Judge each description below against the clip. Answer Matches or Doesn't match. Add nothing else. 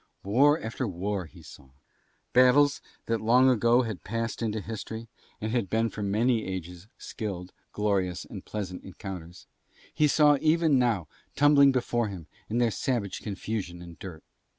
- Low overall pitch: Matches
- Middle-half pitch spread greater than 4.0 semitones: Matches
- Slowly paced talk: Doesn't match